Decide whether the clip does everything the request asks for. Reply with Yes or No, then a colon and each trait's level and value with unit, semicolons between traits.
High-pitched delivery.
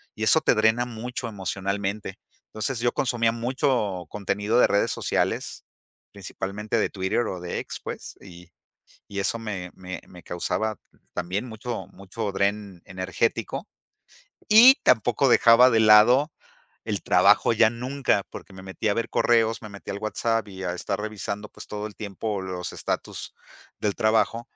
No: low, 105 Hz